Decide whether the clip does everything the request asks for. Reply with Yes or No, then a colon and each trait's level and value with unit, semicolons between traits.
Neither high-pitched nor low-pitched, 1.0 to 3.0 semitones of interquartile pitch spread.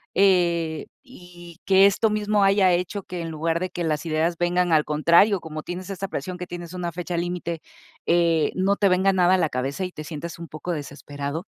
Yes: medium, 175 Hz; narrow, 2.4 semitones